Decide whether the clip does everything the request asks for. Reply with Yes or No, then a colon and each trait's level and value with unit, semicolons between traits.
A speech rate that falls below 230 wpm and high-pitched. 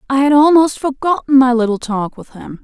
Yes: fast, 205 wpm; very high, 260 Hz